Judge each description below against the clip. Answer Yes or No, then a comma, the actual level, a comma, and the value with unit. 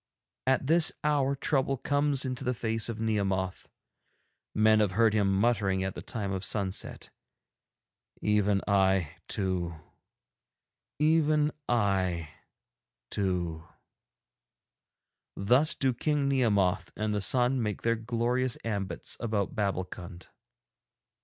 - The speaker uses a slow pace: Yes, slow, 110 wpm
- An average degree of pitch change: Yes, average, 4.9 semitones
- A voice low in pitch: Yes, low, 110 Hz